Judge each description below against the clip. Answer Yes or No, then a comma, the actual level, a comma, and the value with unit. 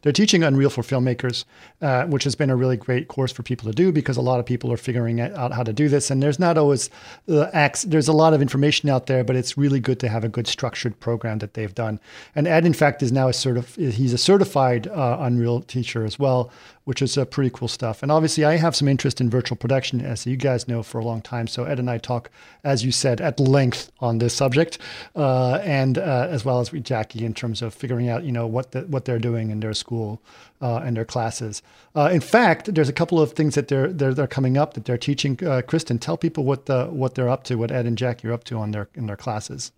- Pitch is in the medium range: No, low, 130 Hz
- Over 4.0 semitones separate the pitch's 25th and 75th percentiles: No, average, 3.1 semitones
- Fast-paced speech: Yes, fast, 260 wpm